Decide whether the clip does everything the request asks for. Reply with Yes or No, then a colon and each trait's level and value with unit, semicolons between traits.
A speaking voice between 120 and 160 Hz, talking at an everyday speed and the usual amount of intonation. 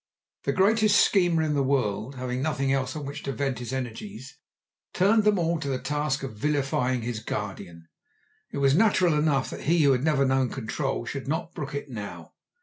Yes: medium, 140 Hz; average, 195 wpm; average, 3.4 semitones